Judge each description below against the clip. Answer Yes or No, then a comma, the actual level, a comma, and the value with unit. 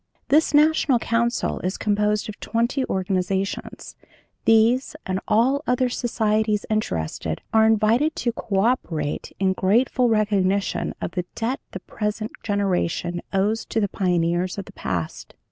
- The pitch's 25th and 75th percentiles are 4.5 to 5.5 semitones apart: No, average, 3.7 semitones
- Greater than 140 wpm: No, slow, 135 wpm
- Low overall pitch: No, high, 210 Hz